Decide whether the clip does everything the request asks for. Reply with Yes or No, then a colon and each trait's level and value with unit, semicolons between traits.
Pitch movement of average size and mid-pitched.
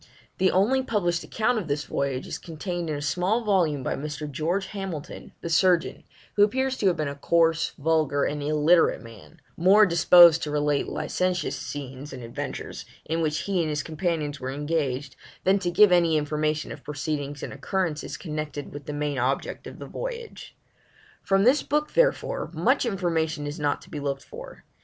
Yes: average, 4.3 semitones; medium, 160 Hz